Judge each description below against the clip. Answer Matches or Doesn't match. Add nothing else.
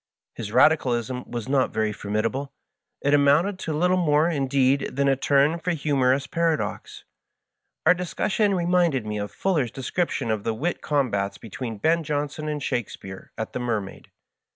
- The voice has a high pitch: Doesn't match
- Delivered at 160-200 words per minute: Doesn't match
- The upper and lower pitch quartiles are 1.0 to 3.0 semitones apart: Doesn't match